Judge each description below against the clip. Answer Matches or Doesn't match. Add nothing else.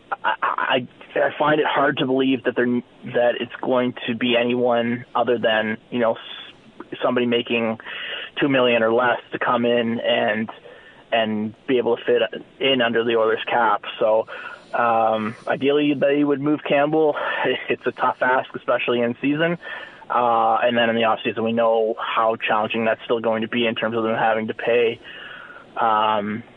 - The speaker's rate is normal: Matches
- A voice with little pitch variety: Matches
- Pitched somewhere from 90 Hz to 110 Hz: Doesn't match